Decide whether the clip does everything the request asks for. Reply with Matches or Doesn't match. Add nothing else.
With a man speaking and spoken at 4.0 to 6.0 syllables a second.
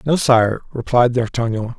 Matches